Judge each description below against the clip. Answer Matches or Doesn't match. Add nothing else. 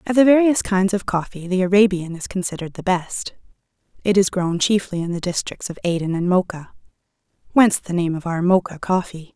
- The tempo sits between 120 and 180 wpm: Doesn't match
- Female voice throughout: Matches